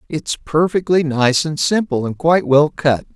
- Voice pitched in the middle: Yes, medium, 155 Hz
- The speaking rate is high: No, average, 170 wpm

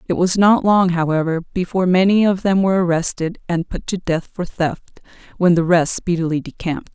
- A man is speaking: No, female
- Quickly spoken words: No, average, 190 wpm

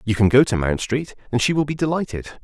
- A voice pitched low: Yes, low, 125 Hz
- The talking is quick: Yes, fast, 270 wpm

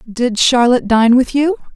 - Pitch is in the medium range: No, very high, 250 Hz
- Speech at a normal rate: Yes, average, 170 wpm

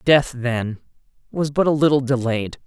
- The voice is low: Yes, low, 130 Hz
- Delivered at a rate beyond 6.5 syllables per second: No, 4.5 syllables/s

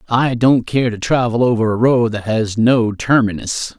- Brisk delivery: No, average, 190 wpm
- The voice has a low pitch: Yes, low, 115 Hz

